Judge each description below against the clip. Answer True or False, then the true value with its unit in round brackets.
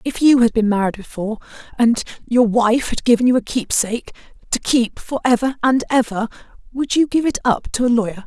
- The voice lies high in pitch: True (235 Hz)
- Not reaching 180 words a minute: False (195 wpm)